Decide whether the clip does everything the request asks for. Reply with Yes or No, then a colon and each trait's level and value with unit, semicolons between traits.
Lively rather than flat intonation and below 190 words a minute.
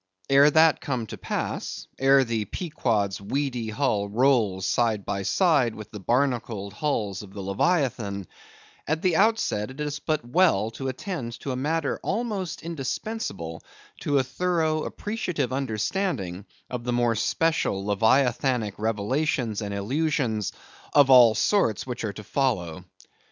Yes: wide, 6.1 semitones; average, 140 wpm